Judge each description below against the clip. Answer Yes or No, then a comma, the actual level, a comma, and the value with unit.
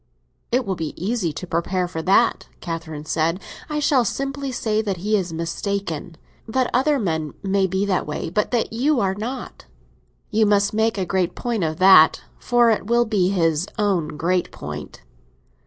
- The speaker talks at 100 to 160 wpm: No, average, 175 wpm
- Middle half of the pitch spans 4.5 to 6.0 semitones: Yes, average, 5.1 semitones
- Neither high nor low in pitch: No, high, 195 Hz